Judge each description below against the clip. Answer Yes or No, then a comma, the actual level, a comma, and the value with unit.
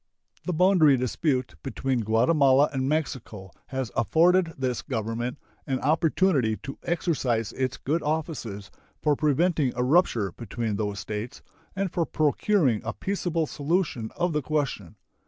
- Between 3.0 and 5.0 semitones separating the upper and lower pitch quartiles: No, wide, 5.6 semitones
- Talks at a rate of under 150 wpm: Yes, slow, 135 wpm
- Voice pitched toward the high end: No, low, 135 Hz